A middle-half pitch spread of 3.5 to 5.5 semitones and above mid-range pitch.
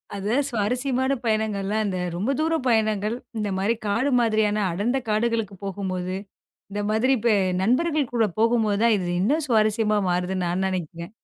No: average, 3.1 semitones; high, 215 Hz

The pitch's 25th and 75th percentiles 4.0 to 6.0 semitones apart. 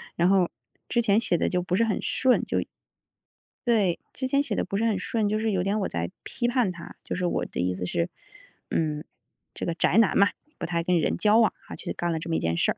Yes: average, 4.7 semitones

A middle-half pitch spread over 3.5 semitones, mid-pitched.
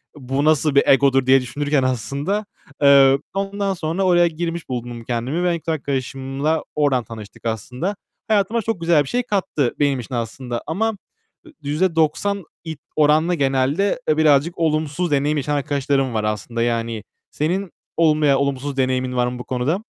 Yes: average, 4.4 semitones; medium, 145 Hz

